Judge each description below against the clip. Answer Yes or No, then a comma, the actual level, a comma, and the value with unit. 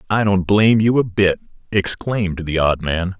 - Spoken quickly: No, average, 190 wpm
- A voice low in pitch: Yes, very low, 95 Hz